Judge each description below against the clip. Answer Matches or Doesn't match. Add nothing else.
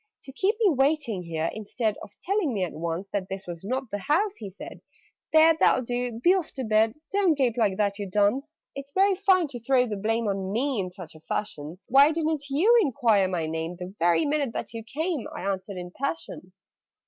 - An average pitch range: Doesn't match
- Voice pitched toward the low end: Doesn't match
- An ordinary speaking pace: Doesn't match